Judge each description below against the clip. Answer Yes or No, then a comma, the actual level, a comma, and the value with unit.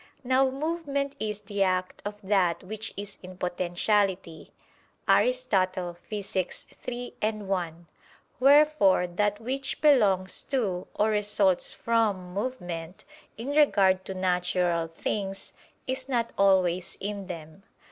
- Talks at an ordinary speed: No, slow, 115 wpm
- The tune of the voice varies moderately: Yes, average, 4.3 semitones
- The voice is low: No, high, 200 Hz